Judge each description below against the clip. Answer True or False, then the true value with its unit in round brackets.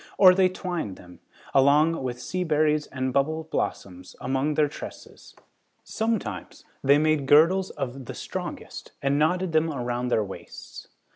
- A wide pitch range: False (4.1 semitones)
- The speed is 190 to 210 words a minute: False (145 wpm)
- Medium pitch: True (150 Hz)